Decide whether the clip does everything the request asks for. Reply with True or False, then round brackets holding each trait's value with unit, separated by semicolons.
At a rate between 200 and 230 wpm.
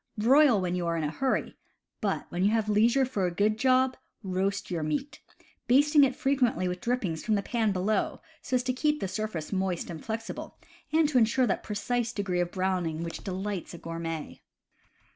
False (190 wpm)